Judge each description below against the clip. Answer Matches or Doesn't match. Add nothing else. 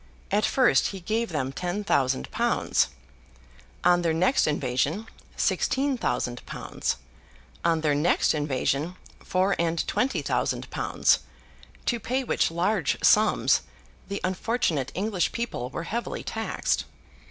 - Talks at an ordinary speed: Doesn't match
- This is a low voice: Doesn't match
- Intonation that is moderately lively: Doesn't match